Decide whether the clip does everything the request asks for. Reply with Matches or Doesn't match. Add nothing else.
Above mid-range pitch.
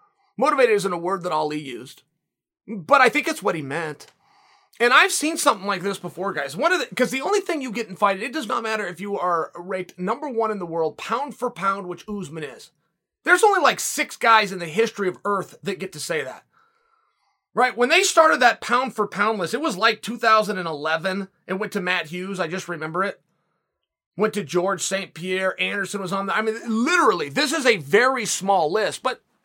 Matches